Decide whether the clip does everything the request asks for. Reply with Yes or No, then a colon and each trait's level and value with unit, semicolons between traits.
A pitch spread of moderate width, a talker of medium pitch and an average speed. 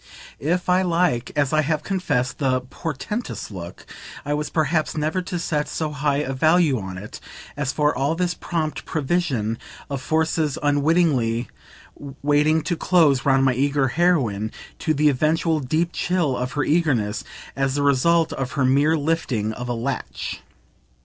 Yes: average, 3.8 semitones; medium, 145 Hz; average, 160 wpm